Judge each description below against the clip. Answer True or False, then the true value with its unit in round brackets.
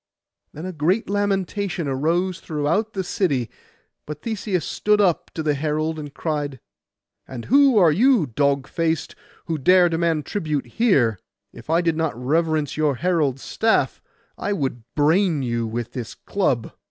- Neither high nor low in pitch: True (160 Hz)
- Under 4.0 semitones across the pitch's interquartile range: False (4.8 semitones)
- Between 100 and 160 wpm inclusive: True (155 wpm)